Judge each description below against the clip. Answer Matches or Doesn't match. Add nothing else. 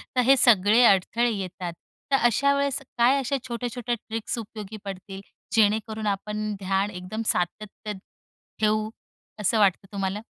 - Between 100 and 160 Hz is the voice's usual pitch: Doesn't match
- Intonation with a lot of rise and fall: Doesn't match